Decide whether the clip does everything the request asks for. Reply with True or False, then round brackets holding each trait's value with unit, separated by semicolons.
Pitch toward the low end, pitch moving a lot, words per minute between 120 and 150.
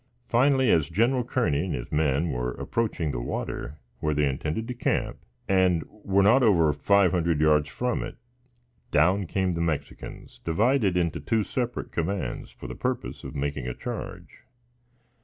False (85 Hz; 6.2 semitones; 160 wpm)